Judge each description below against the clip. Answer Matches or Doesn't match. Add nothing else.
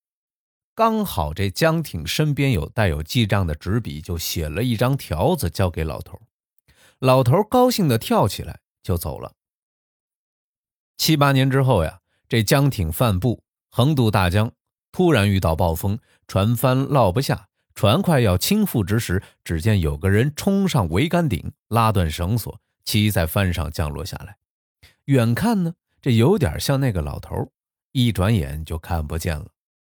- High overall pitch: Doesn't match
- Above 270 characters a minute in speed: Doesn't match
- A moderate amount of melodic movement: Doesn't match